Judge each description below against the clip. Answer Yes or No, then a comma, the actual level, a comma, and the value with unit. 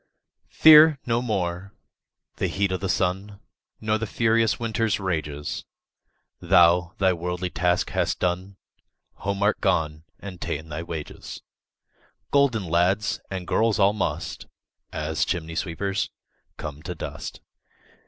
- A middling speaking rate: No, slow, 130 wpm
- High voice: No, very low, 95 Hz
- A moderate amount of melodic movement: Yes, average, 3.7 semitones